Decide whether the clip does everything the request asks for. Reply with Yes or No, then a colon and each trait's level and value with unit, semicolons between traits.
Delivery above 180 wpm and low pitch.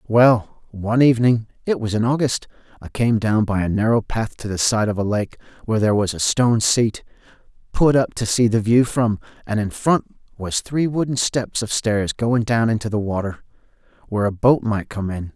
Yes: average, 200 wpm; low, 110 Hz